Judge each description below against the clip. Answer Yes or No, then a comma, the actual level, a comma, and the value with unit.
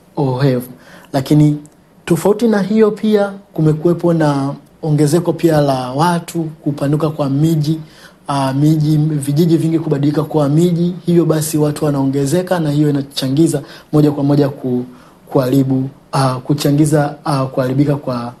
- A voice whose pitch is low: No, medium, 150 Hz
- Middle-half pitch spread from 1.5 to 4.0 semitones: Yes, average, 2.8 semitones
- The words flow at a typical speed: Yes, average, 125 wpm